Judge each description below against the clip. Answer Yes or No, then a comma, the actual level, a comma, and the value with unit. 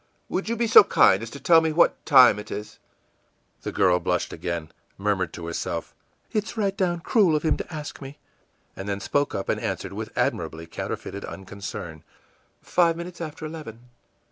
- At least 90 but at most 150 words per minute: No, average, 185 wpm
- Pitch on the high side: No, low, 135 Hz